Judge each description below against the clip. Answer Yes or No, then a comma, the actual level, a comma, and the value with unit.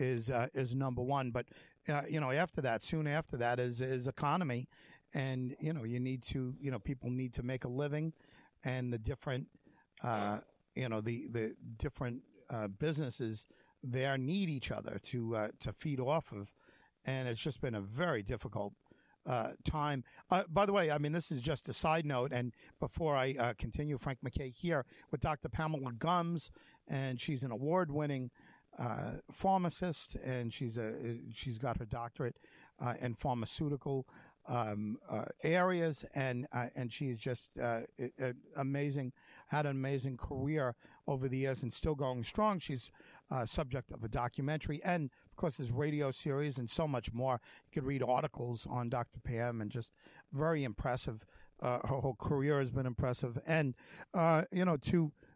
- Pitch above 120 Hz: Yes, low, 135 Hz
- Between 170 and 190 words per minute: Yes, average, 180 wpm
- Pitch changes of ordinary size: Yes, average, 3.5 semitones